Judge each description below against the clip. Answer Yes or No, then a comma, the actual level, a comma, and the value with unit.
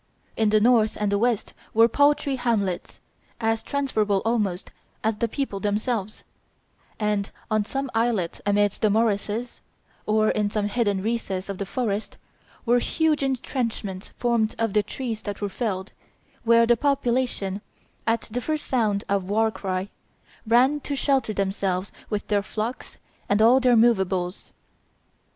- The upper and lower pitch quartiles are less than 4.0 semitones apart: Yes, average, 3.0 semitones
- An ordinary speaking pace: Yes, average, 150 wpm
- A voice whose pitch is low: No, high, 220 Hz